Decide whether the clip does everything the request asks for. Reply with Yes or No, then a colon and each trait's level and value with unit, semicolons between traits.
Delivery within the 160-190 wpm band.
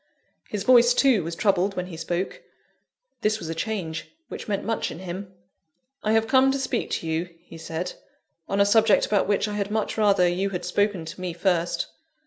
No: average, 200 wpm